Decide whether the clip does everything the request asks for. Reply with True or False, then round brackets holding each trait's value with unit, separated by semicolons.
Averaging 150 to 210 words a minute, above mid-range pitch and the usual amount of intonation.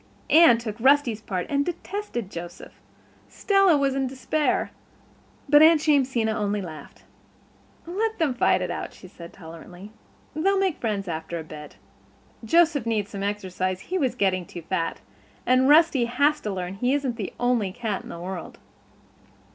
False (155 wpm; 230 Hz; 7.6 semitones)